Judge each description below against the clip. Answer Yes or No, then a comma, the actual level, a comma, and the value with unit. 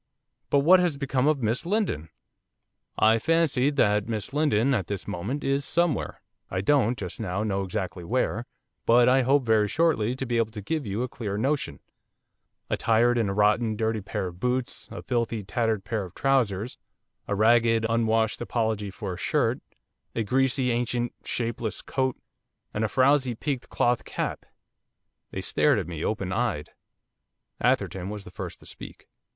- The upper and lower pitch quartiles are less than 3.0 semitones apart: No, average, 3.9 semitones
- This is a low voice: Yes, low, 115 Hz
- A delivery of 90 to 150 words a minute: No, average, 170 wpm